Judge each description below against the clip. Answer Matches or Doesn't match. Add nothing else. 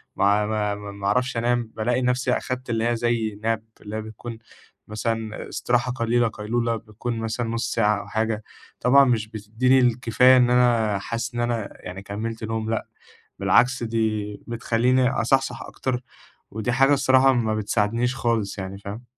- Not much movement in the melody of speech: Matches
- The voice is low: Matches